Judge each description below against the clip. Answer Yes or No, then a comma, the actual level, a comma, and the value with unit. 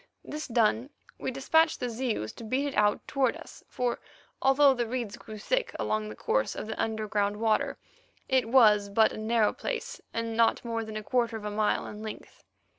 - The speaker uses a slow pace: No, average, 195 wpm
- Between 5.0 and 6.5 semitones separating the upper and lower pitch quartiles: No, average, 3.2 semitones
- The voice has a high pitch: Yes, high, 225 Hz